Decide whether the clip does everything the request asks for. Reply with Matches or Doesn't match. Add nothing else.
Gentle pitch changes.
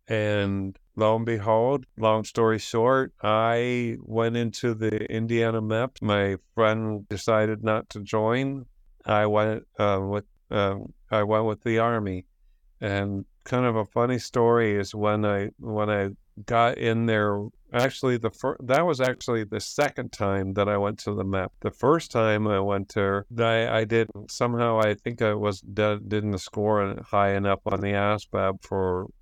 Matches